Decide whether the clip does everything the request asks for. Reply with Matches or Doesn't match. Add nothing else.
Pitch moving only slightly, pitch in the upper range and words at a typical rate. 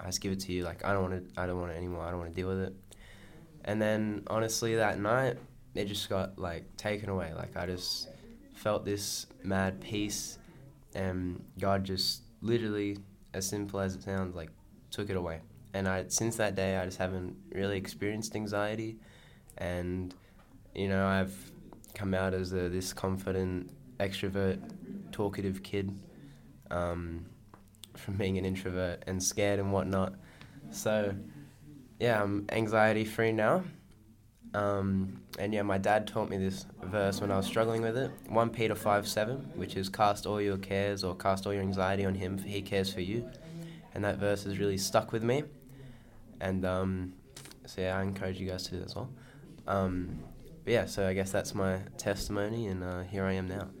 Doesn't match